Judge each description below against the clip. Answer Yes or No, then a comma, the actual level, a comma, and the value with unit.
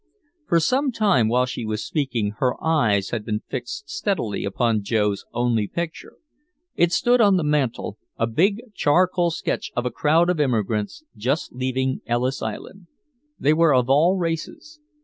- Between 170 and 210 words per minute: No, average, 160 wpm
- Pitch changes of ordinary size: No, wide, 7.1 semitones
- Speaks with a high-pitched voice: No, medium, 140 Hz